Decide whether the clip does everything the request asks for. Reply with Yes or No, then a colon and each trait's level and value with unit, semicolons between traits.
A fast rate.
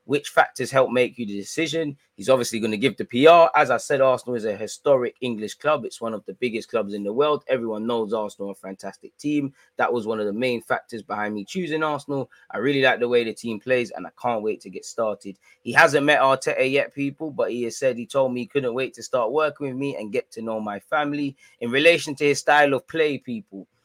Yes: fast, 250 wpm